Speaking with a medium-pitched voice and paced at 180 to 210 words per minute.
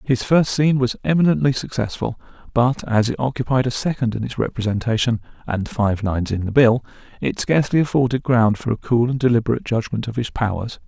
No: low, 120 Hz; average, 190 wpm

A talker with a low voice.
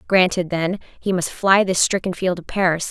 No: medium, 185 Hz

